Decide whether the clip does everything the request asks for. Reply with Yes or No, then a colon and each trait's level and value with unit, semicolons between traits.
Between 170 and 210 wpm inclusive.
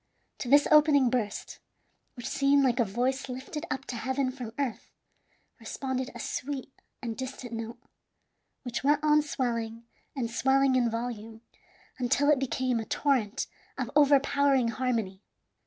No: average, 140 wpm